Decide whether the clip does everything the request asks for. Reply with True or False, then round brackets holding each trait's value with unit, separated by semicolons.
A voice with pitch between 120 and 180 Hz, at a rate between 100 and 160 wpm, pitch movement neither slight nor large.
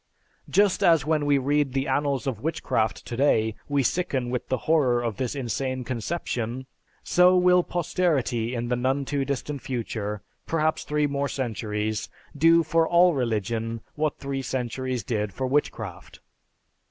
True (135 Hz; 150 wpm; 4.0 semitones)